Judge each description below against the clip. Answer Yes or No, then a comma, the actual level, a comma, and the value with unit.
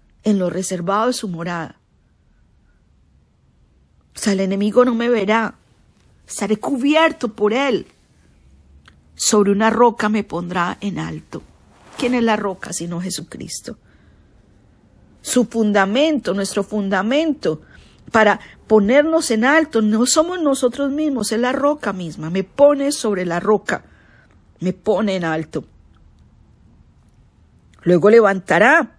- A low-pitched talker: No, high, 205 Hz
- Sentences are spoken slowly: Yes, slow, 120 wpm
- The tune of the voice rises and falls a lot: Yes, wide, 6.6 semitones